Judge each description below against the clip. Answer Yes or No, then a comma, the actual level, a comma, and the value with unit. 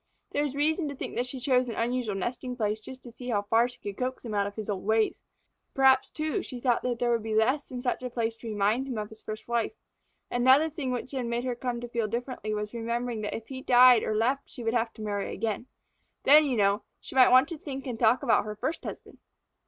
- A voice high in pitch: Yes, high, 240 Hz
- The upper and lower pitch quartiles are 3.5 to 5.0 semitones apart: No, average, 2.9 semitones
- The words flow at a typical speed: No, fast, 255 wpm